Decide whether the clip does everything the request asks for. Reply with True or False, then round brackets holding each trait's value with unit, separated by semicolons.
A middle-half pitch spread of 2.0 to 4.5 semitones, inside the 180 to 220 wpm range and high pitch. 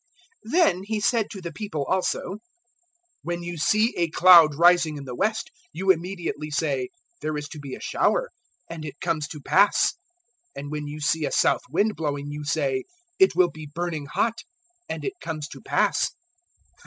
False (4.2 semitones; 185 wpm; 165 Hz)